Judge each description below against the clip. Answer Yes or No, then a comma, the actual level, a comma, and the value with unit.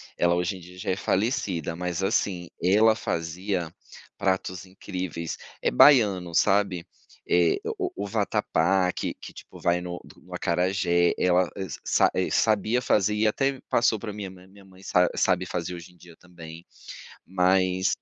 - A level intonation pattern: Yes, narrow, 2.2 semitones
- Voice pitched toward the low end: Yes, very low, 95 Hz